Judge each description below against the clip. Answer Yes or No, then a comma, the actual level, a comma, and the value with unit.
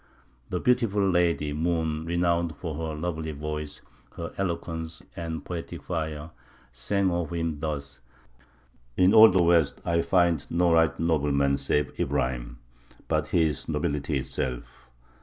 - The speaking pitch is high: No, very low, 80 Hz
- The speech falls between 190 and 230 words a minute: No, average, 140 wpm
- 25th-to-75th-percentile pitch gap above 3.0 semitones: No, narrow, 2.6 semitones